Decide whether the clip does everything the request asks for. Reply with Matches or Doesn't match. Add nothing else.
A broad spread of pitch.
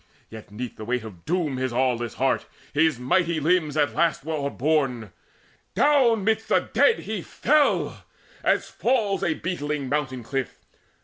Matches